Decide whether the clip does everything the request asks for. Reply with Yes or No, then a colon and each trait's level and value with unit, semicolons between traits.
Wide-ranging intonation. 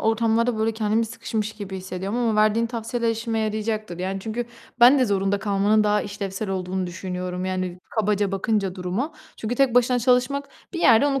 No: average, 3.2 semitones